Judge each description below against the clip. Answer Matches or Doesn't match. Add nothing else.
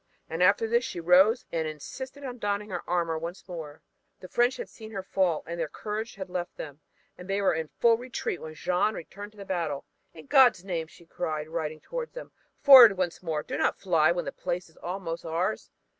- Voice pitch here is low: Doesn't match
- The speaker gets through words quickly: Matches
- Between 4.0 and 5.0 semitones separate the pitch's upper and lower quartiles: Matches